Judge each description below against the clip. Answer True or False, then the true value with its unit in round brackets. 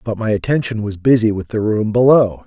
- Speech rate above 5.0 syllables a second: True (5.5 syllables/s)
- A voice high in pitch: False (110 Hz)